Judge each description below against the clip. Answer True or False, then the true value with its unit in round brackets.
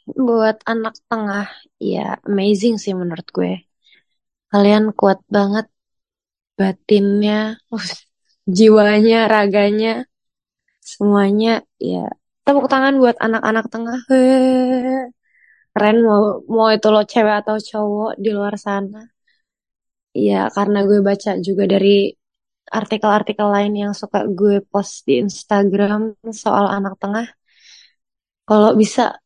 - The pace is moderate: True (105 wpm)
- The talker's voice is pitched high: True (215 Hz)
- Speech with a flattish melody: True (1.8 semitones)